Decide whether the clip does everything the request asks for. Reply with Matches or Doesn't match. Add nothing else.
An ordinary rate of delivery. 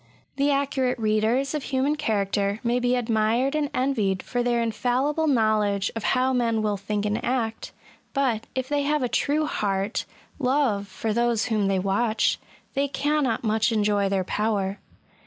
Matches